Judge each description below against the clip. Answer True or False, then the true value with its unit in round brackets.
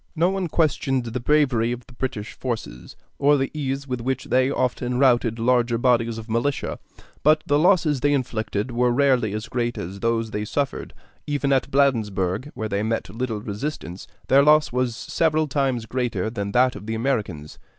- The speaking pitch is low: True (125 Hz)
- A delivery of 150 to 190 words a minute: True (180 wpm)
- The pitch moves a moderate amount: True (3.7 semitones)